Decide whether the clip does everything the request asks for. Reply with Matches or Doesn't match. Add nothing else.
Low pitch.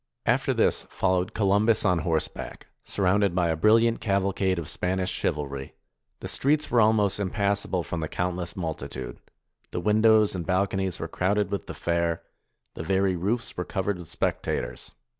Matches